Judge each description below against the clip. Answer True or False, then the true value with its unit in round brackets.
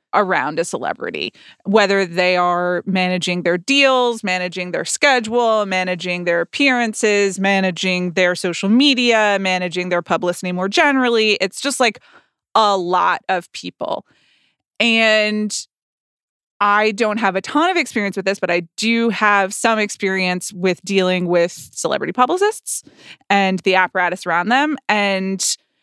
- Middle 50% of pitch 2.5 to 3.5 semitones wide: False (3.9 semitones)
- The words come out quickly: False (135 wpm)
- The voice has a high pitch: True (195 Hz)